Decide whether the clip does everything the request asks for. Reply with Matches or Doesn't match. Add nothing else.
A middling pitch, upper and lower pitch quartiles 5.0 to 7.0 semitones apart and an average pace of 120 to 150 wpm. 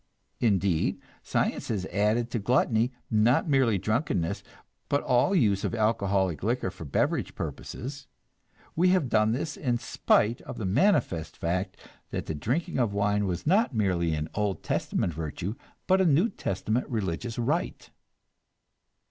Doesn't match